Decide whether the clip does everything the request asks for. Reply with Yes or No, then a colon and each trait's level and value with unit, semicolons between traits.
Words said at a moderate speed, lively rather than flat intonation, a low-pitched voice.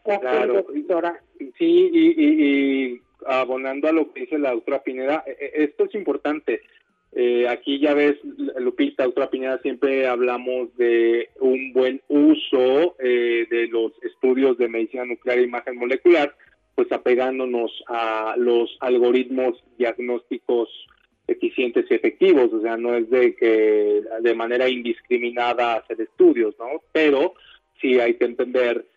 Yes: average, 135 wpm; wide, 6.1 semitones; low, 130 Hz